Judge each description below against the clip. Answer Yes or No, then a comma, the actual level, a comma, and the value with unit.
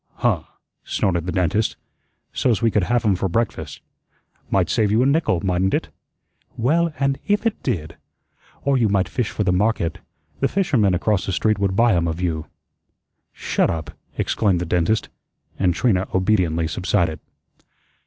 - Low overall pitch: Yes, low, 100 Hz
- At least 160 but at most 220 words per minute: Yes, average, 165 wpm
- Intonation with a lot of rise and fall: No, average, 4.6 semitones